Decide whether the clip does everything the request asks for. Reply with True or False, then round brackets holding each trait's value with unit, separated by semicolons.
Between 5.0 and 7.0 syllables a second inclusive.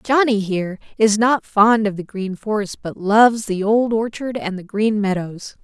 False (4.6 syllables/s)